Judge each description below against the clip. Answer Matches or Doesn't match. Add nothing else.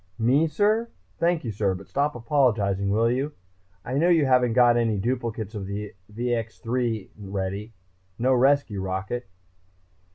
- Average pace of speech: Matches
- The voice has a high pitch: Doesn't match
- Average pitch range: Matches